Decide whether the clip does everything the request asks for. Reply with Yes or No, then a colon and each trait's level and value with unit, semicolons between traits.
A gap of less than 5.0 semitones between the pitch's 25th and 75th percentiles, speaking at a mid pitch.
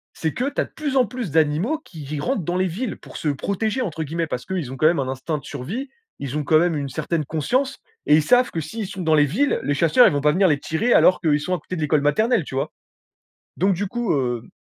No: wide, 6.2 semitones; medium, 165 Hz